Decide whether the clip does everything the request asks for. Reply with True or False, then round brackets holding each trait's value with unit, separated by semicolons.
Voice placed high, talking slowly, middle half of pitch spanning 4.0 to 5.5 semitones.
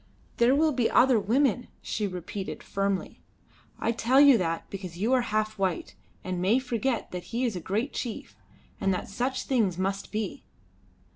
False (215 Hz; 170 wpm; 4.4 semitones)